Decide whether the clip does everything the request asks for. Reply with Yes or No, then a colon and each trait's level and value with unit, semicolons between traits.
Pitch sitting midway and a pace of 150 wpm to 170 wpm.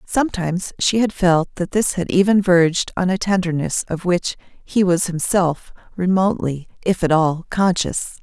Yes: medium, 180 Hz; average, 160 wpm